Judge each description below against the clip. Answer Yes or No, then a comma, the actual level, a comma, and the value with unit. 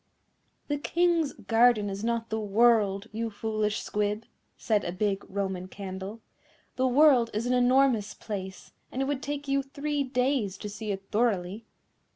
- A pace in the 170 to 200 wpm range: No, average, 160 wpm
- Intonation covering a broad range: No, average, 4.3 semitones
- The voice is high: Yes, high, 225 Hz